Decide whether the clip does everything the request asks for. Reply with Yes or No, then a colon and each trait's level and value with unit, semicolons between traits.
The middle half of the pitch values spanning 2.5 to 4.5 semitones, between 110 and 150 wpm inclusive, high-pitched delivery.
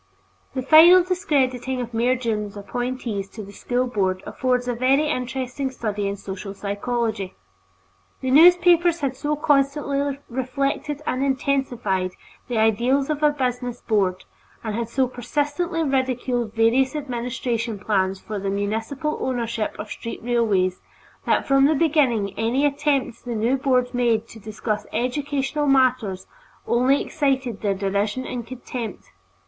Yes: average, 3.9 semitones; average, 140 wpm; very high, 250 Hz